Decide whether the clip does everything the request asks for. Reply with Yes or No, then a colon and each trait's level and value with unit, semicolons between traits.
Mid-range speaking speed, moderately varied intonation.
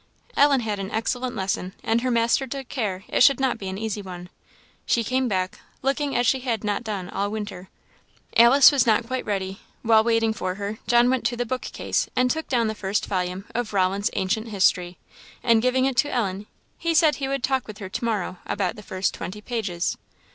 No: fast, 210 wpm; average, 4.3 semitones